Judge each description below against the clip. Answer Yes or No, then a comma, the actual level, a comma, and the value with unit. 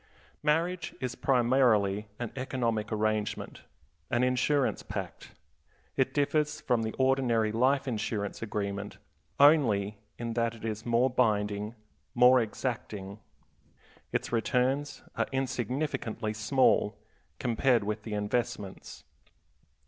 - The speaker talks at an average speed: No, slow, 105 wpm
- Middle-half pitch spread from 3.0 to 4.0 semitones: Yes, average, 3.5 semitones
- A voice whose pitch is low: Yes, low, 120 Hz